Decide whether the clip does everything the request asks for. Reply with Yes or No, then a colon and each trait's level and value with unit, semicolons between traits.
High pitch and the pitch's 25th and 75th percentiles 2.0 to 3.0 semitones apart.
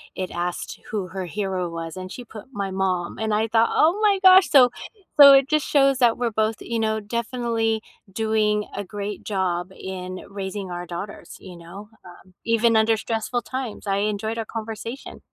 No: high, 215 Hz; average, 3.4 semitones